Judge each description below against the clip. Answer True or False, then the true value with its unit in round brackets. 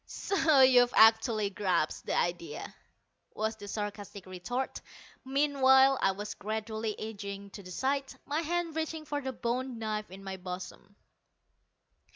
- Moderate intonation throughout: True (5.0 semitones)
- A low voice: False (220 Hz)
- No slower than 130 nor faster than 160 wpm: True (140 wpm)